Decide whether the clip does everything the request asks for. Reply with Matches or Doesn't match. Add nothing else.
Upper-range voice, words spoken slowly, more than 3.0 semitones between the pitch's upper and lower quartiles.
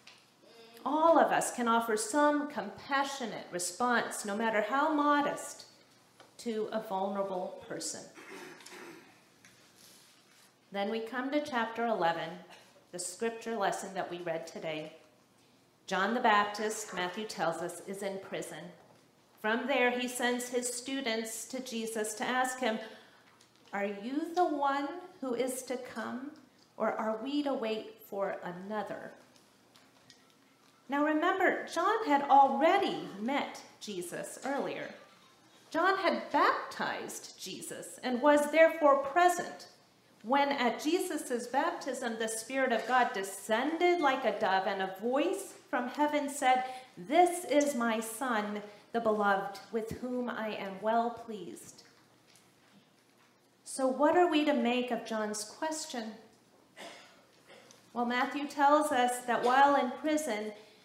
Matches